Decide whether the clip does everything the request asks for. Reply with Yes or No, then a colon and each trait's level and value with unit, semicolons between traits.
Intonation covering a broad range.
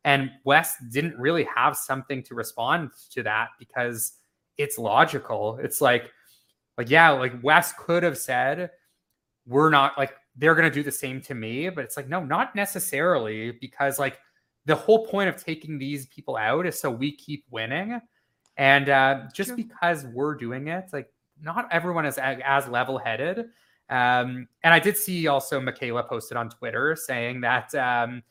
No: average, 4.5 semitones